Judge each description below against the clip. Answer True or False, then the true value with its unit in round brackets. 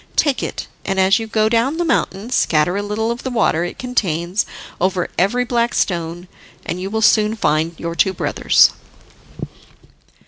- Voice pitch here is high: True (205 Hz)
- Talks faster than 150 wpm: True (170 wpm)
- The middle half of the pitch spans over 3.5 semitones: True (5.0 semitones)